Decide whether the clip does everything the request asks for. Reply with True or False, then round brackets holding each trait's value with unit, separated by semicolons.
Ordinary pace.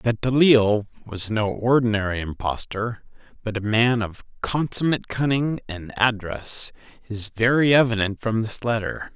False (130 wpm)